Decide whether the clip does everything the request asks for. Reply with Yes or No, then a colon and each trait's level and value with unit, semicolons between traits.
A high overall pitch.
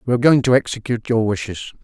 No: low, 120 Hz